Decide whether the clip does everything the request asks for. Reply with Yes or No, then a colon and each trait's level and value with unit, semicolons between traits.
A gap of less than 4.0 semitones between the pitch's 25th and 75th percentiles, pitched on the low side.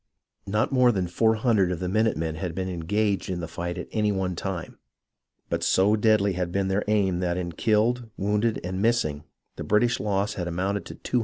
Yes: average, 3.1 semitones; low, 100 Hz